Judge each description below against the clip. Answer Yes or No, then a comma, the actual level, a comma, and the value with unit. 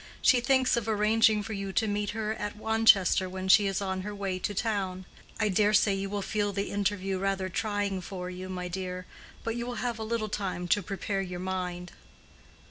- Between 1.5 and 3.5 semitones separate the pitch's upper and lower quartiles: Yes, narrow, 2.4 semitones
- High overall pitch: Yes, high, 200 Hz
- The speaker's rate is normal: No, fast, 210 wpm